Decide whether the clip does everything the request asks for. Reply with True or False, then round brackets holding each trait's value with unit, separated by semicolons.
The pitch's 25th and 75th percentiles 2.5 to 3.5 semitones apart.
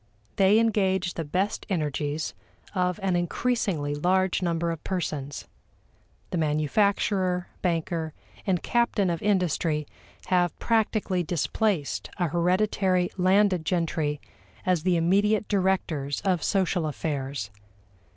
True (3.2 semitones)